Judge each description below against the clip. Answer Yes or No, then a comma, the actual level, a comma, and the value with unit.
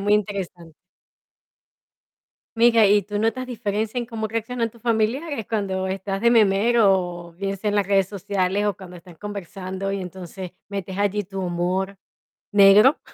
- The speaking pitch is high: Yes, high, 200 Hz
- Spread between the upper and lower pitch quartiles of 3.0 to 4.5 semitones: No, narrow, 2.6 semitones